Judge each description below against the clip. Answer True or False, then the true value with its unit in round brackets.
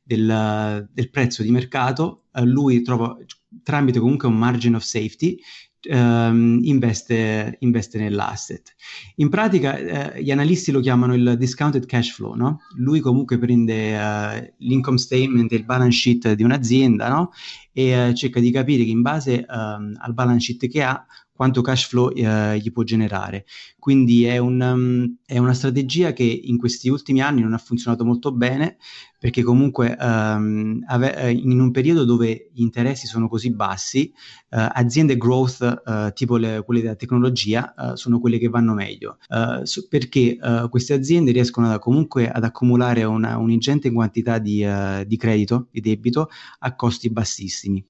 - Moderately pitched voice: False (120 Hz)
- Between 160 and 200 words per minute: True (165 wpm)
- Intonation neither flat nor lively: False (2.1 semitones)